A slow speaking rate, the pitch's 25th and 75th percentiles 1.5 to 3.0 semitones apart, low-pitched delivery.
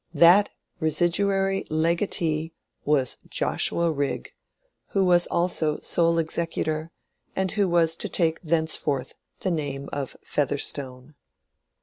No: slow, 105 wpm; narrow, 2.6 semitones; medium, 165 Hz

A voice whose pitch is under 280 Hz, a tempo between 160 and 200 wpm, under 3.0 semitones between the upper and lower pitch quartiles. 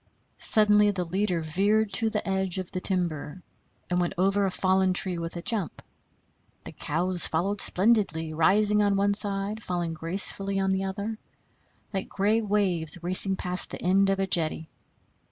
Yes: high, 190 Hz; average, 170 wpm; narrow, 2.4 semitones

